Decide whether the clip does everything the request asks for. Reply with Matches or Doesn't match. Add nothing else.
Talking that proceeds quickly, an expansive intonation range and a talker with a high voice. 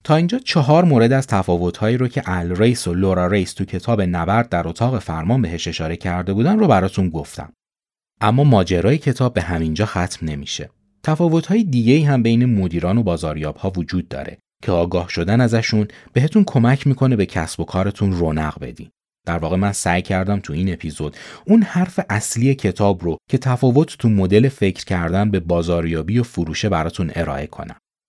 Doesn't match